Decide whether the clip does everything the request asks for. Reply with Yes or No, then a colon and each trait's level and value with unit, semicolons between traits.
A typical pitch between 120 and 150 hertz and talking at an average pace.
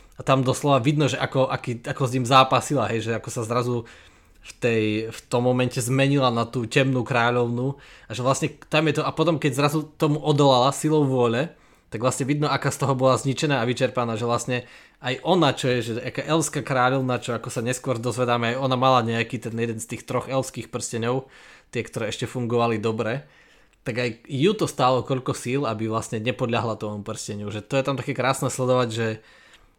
No: low, 125 Hz; fast, 205 wpm